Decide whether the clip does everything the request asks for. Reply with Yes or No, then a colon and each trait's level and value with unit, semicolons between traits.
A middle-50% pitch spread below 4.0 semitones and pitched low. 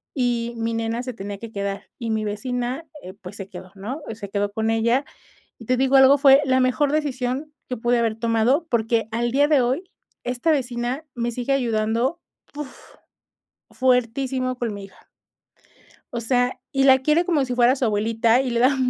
No: average, 2.8 semitones; high, 245 Hz